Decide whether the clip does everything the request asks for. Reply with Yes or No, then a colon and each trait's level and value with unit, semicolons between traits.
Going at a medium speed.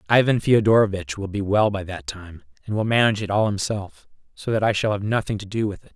No: fast, 240 wpm